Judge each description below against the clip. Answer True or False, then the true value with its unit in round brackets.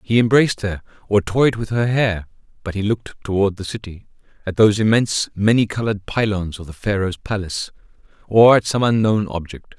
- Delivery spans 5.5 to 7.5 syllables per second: True (5.7 syllables/s)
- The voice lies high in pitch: False (105 Hz)